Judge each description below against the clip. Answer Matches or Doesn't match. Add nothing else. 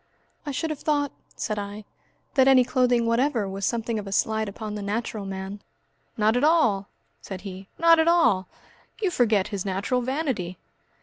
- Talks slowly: Doesn't match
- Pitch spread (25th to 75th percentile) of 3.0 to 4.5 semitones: Doesn't match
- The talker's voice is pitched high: Matches